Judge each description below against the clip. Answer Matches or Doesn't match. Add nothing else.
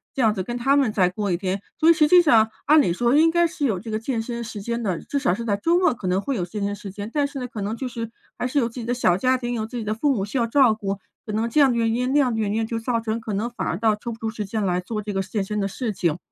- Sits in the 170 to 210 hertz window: Doesn't match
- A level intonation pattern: Doesn't match